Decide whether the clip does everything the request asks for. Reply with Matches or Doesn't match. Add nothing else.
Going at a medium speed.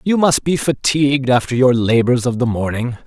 Matches